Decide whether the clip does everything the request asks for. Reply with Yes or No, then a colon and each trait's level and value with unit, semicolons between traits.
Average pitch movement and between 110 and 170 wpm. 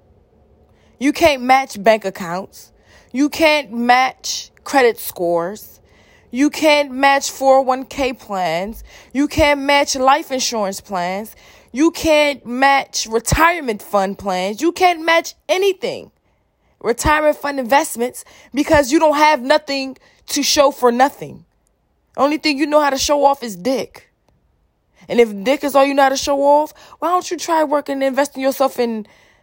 Yes: average, 3.9 semitones; average, 150 wpm